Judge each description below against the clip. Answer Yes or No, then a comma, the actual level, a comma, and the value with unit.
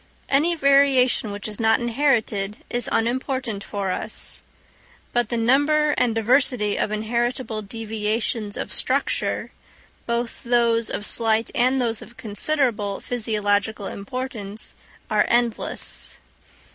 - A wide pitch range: No, average, 2.9 semitones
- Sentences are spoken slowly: Yes, slow, 115 wpm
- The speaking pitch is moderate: No, high, 230 Hz